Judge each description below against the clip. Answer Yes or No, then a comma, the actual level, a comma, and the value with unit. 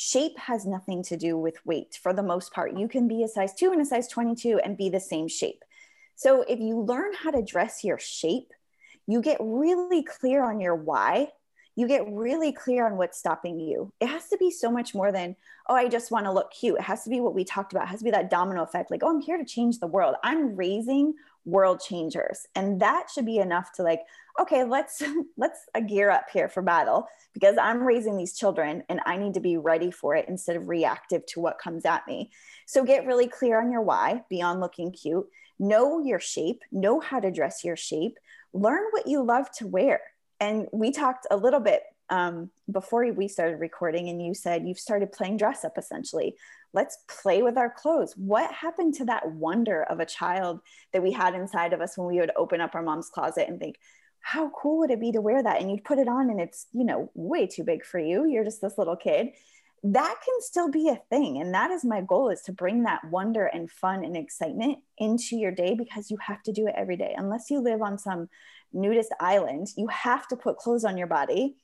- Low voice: No, high, 225 Hz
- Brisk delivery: Yes, fast, 230 wpm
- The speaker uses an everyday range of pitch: No, wide, 7.1 semitones